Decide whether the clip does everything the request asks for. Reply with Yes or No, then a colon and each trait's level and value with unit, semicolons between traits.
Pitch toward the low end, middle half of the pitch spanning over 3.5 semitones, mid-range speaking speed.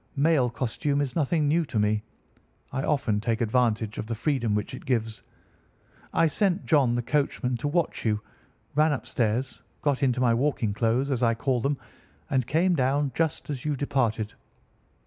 Yes: low, 130 Hz; average, 4.1 semitones; average, 170 wpm